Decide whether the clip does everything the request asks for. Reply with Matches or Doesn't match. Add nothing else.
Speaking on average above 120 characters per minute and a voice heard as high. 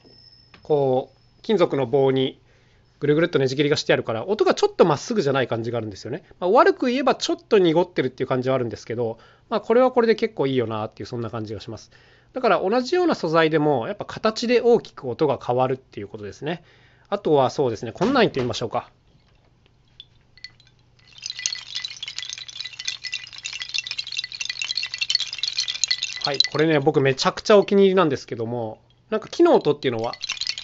Doesn't match